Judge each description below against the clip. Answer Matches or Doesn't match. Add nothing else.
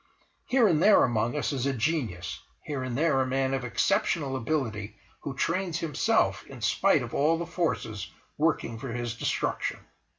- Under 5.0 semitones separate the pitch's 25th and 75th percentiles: Doesn't match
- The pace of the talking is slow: Doesn't match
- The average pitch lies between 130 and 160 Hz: Matches